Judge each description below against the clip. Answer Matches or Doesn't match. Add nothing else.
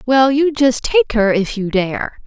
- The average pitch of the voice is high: Matches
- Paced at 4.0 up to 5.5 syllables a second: Doesn't match